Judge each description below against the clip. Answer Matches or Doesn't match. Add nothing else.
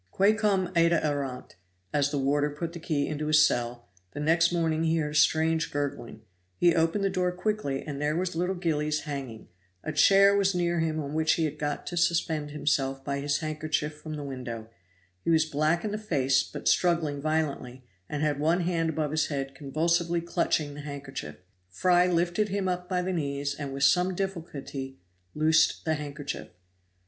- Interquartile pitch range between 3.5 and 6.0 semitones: Doesn't match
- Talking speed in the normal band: Matches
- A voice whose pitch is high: Doesn't match